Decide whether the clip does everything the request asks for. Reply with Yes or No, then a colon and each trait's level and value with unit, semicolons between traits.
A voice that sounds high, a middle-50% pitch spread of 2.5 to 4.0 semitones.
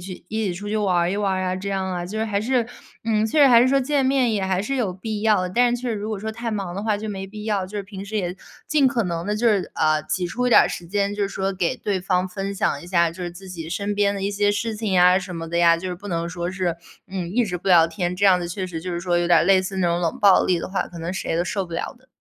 Yes: high, 195 Hz; average, 3.0 semitones